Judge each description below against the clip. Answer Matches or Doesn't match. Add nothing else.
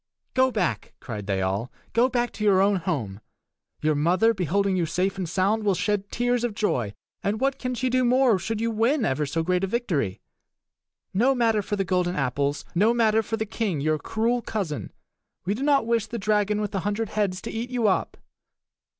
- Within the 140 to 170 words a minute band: Doesn't match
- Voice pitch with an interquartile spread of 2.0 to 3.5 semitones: Doesn't match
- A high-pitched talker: Matches